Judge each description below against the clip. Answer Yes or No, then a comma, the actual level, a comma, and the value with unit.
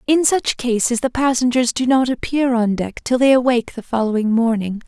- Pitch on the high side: Yes, high, 245 Hz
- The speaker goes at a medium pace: Yes, average, 195 wpm